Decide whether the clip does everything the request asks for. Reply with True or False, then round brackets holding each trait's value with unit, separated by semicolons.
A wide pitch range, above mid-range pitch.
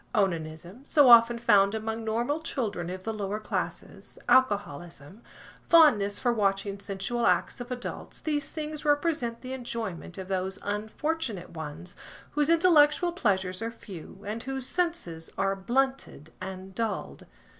True (5.7 semitones; 220 Hz)